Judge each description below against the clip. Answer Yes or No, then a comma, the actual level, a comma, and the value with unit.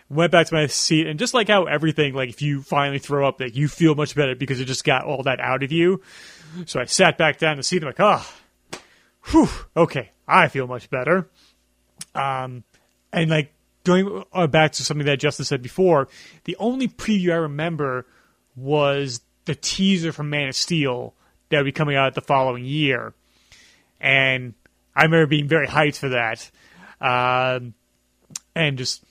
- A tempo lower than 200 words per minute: Yes, average, 185 wpm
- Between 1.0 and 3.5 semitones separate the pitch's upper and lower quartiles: No, average, 3.9 semitones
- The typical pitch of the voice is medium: Yes, medium, 145 Hz